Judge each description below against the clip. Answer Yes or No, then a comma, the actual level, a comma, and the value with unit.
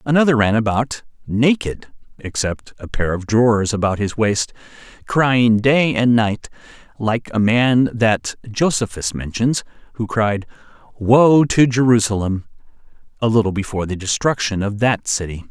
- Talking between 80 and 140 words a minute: Yes, slow, 135 wpm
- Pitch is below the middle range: Yes, low, 115 Hz